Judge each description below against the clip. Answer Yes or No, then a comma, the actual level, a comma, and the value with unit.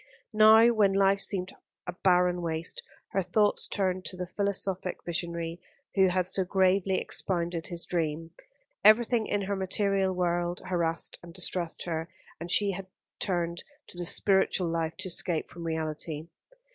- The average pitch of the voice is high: No, medium, 180 Hz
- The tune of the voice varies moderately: No, narrow, 2.3 semitones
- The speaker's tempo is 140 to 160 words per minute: Yes, average, 145 wpm